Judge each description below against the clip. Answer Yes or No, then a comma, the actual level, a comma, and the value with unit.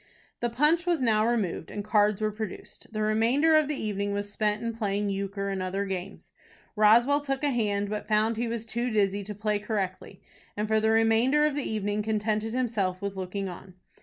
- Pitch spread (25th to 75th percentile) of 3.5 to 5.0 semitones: No, narrow, 2.4 semitones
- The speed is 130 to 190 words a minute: No, average, 200 wpm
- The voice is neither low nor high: No, high, 215 Hz